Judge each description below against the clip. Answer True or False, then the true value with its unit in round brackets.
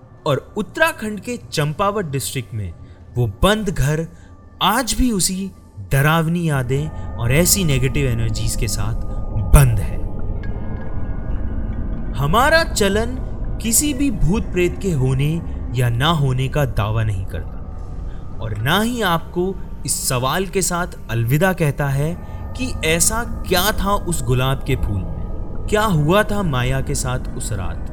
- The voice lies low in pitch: True (130 Hz)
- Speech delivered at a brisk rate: False (140 wpm)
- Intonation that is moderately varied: False (9.0 semitones)